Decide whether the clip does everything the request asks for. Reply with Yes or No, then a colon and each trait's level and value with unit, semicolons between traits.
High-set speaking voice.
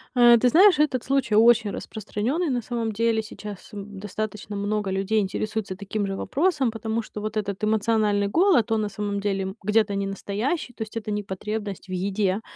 Yes: high, 215 Hz